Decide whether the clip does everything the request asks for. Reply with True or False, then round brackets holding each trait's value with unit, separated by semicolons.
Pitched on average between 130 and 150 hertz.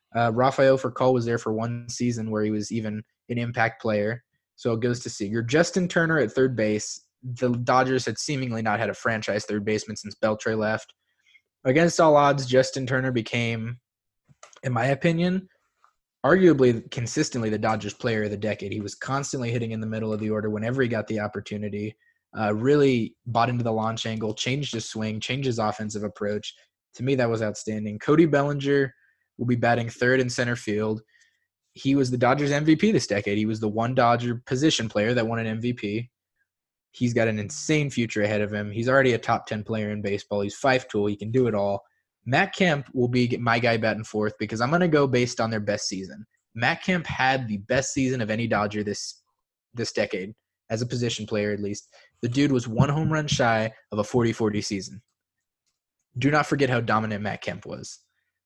False (115 Hz)